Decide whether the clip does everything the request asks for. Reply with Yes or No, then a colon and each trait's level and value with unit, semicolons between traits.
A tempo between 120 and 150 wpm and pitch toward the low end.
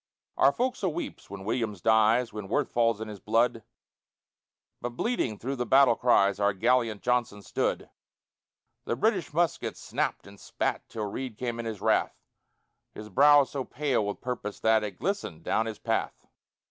No: average, 165 wpm; low, 115 Hz